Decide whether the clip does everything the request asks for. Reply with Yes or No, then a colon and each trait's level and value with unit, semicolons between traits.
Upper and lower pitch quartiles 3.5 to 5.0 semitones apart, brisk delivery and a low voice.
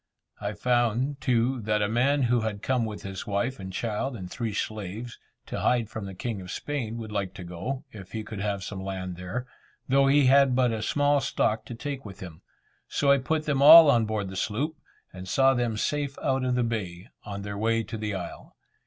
Yes: average, 4.6 semitones; fast, 220 wpm; low, 115 Hz